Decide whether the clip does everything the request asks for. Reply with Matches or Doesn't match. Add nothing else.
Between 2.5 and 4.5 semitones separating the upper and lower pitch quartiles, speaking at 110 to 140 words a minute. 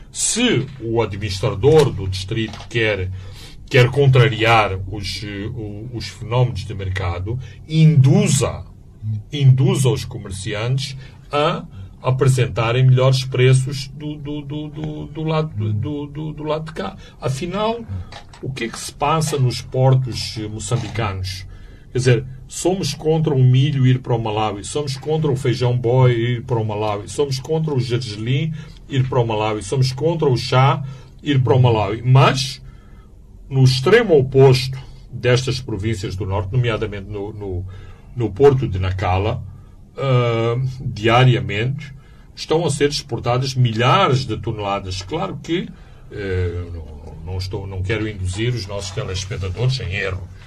Matches